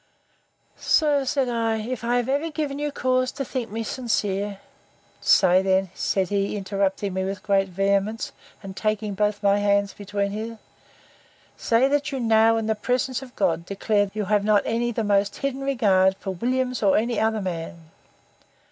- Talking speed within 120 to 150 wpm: No, average, 175 wpm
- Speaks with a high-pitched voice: Yes, high, 215 Hz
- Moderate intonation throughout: Yes, average, 3.8 semitones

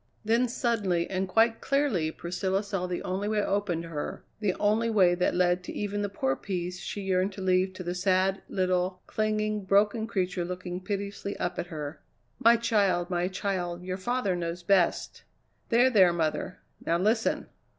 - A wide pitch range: No, average, 2.7 semitones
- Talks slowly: No, average, 175 wpm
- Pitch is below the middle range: No, high, 190 Hz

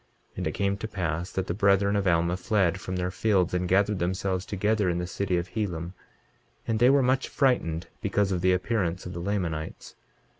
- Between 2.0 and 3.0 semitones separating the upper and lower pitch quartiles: Yes, narrow, 2.6 semitones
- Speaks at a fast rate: Yes, fast, 210 wpm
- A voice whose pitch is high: No, very low, 95 Hz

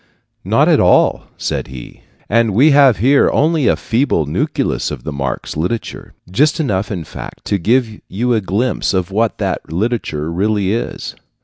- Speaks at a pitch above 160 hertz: No, low, 105 Hz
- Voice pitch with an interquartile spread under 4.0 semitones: No, wide, 5.5 semitones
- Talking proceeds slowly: No, average, 170 wpm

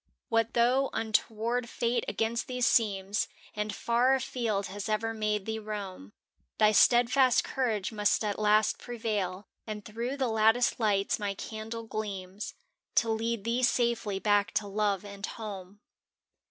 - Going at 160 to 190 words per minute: No, average, 150 wpm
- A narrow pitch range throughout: Yes, narrow, 2.3 semitones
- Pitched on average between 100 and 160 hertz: No, high, 220 Hz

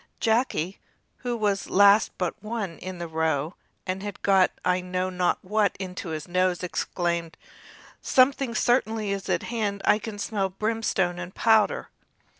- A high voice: Yes, high, 195 Hz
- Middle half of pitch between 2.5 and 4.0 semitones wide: Yes, average, 3.3 semitones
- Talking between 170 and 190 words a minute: No, average, 155 wpm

